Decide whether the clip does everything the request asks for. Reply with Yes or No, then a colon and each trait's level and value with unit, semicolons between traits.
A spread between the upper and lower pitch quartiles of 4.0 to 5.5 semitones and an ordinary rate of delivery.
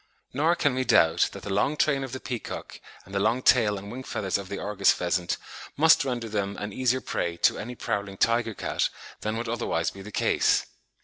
No: average, 4.3 semitones; fast, 210 wpm